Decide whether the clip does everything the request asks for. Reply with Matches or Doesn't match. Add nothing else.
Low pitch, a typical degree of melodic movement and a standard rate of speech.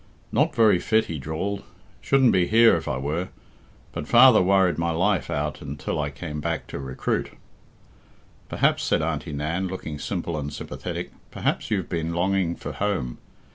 Matches